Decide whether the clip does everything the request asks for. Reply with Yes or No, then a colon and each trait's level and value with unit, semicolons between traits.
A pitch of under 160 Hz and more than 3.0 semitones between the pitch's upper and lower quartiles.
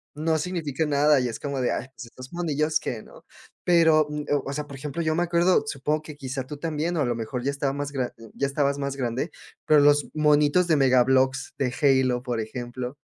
No: medium, 140 Hz; average, 2.7 semitones